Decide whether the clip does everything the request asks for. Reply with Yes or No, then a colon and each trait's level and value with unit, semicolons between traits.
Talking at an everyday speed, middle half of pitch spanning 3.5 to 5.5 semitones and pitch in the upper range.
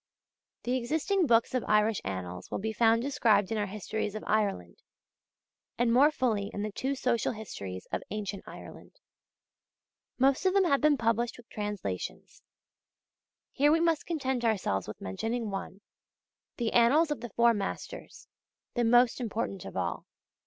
Yes: average, 155 wpm; average, 4.1 semitones; high, 230 Hz